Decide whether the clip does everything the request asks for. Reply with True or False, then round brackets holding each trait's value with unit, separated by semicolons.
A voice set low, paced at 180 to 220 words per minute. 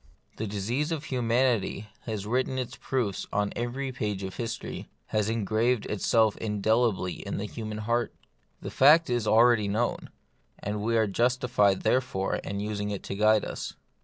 False (110 Hz; 165 wpm)